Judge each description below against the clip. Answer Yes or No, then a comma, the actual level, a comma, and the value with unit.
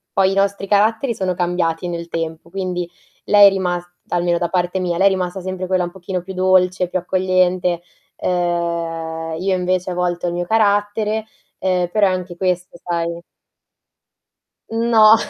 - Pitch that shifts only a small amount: Yes, narrow, 1.7 semitones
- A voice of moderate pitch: Yes, medium, 180 Hz